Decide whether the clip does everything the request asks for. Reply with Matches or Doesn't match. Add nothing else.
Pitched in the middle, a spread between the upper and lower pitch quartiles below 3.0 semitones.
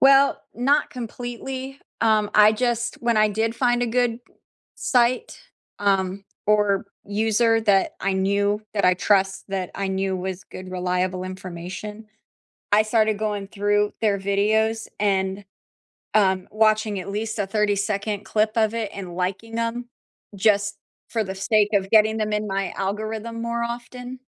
Doesn't match